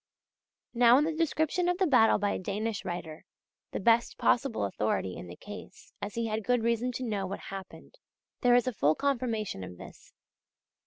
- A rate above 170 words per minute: Yes, average, 190 wpm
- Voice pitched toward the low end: No, high, 225 Hz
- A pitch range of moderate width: Yes, average, 4.5 semitones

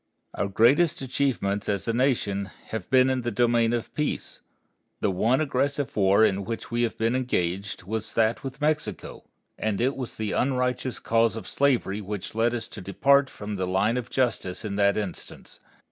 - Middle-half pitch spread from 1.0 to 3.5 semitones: No, average, 4.3 semitones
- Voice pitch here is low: Yes, low, 115 Hz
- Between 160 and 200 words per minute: Yes, average, 180 wpm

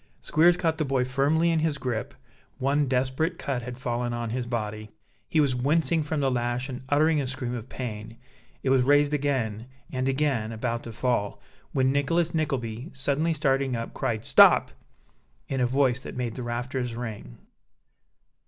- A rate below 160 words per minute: No, average, 170 wpm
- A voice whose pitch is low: Yes, low, 130 Hz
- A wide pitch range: No, average, 3.2 semitones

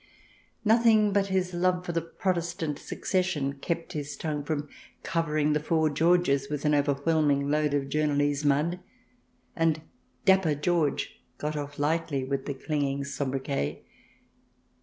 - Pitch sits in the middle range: Yes, medium, 150 Hz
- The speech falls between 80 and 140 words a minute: Yes, slow, 135 wpm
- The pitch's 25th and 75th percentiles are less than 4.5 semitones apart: Yes, average, 3.0 semitones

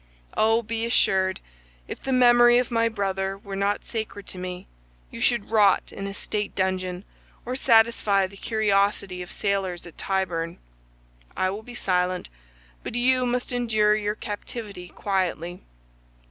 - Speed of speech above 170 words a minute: No, average, 145 wpm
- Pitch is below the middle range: No, high, 200 Hz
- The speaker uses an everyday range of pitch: Yes, average, 3.3 semitones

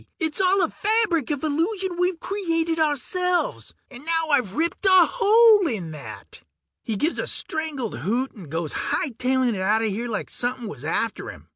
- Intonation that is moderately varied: No, wide, 7.8 semitones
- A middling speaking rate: Yes, average, 165 wpm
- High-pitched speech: Yes, very high, 305 Hz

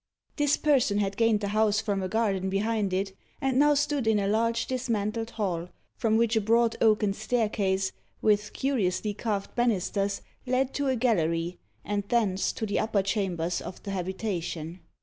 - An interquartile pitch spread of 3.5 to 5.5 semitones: No, average, 3.0 semitones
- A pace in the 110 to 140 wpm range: No, average, 170 wpm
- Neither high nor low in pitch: No, high, 210 Hz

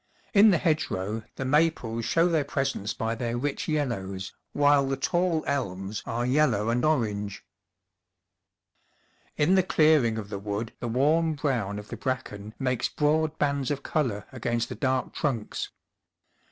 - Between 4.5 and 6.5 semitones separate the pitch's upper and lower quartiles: Yes, wide, 5.4 semitones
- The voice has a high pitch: No, low, 130 Hz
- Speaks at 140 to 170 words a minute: Yes, average, 150 wpm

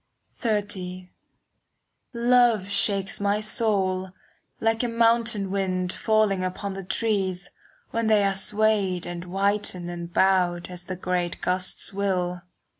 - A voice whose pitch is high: Yes, high, 195 Hz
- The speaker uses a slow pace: Yes, slow, 120 wpm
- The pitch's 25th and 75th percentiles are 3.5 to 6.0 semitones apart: No, average, 2.9 semitones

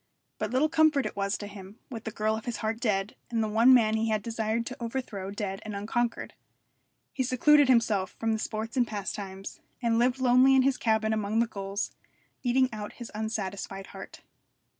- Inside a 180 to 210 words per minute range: Yes, average, 195 wpm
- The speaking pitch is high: Yes, high, 220 Hz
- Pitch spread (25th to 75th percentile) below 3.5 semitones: Yes, average, 2.9 semitones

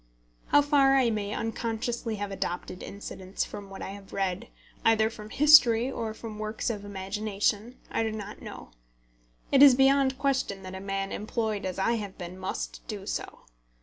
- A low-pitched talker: No, high, 215 Hz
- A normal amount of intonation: Yes, average, 3.3 semitones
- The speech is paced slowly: No, average, 175 wpm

